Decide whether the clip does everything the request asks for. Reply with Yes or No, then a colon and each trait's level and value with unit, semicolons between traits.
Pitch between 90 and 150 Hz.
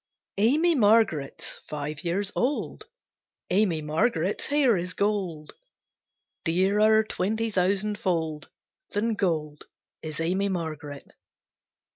No: high, 190 Hz